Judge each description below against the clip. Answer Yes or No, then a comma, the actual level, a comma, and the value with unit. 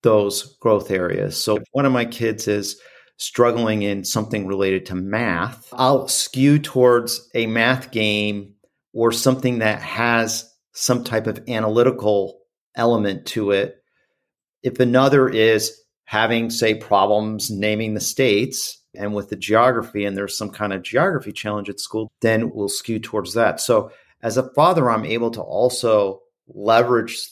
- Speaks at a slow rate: No, average, 150 wpm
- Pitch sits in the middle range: No, low, 110 Hz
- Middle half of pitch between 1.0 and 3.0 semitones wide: Yes, narrow, 2.5 semitones